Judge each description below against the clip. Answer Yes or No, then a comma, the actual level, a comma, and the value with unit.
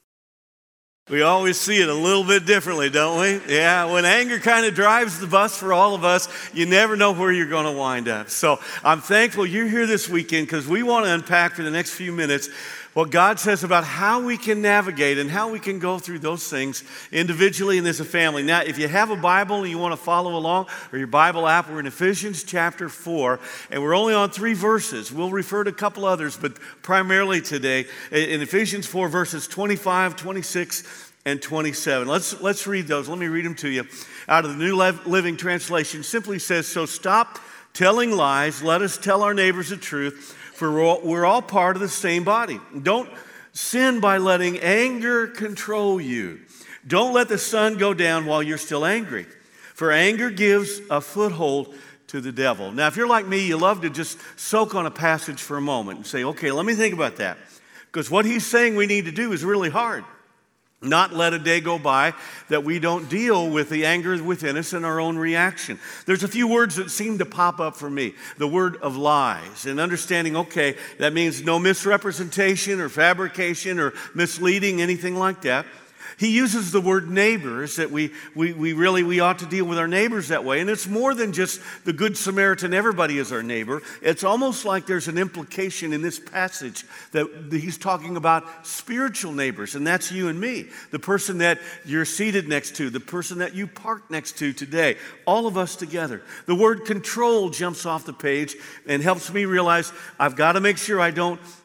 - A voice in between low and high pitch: Yes, medium, 180 Hz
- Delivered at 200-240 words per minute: Yes, fast, 205 wpm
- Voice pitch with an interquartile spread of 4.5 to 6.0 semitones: No, average, 3.8 semitones